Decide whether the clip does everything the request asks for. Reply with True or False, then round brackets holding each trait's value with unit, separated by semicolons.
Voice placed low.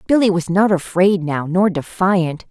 False (185 Hz)